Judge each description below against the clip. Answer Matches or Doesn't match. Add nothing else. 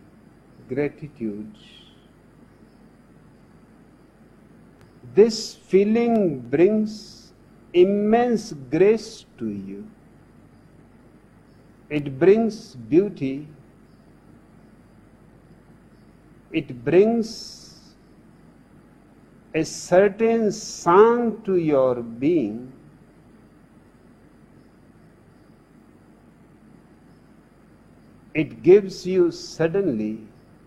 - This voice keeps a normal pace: Doesn't match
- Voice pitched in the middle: Matches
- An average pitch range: Doesn't match